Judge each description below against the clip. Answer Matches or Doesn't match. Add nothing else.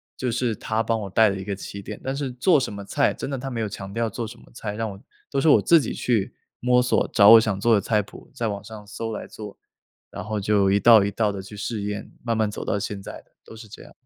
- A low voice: Matches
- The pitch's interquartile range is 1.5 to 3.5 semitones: Matches